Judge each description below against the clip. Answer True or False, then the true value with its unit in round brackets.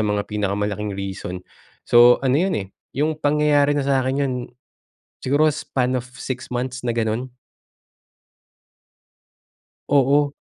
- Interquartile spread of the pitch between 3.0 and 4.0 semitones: False (5.1 semitones)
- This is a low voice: True (130 Hz)